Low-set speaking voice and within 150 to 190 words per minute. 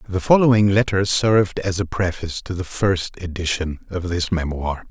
Yes: very low, 95 Hz; average, 170 wpm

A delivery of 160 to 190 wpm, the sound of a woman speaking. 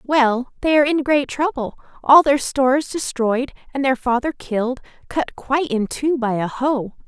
Yes: average, 170 wpm; female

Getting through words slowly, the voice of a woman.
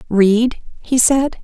Yes: slow, 125 wpm; female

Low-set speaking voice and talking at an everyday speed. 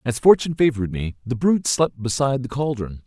Yes: low, 130 Hz; average, 195 wpm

